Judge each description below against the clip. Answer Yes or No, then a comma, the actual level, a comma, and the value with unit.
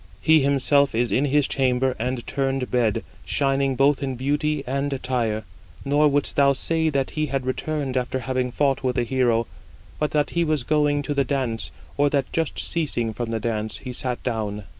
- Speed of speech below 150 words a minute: No, average, 190 wpm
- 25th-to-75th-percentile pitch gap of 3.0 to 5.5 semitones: No, narrow, 2.6 semitones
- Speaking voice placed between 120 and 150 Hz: Yes, low, 135 Hz